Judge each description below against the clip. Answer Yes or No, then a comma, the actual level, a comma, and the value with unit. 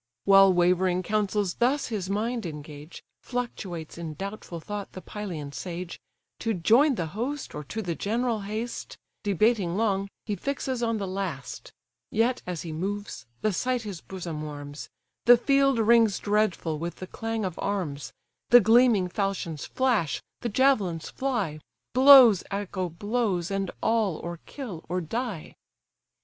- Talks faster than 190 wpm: No, average, 145 wpm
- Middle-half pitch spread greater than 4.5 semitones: Yes, average, 4.9 semitones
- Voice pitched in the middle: No, high, 200 Hz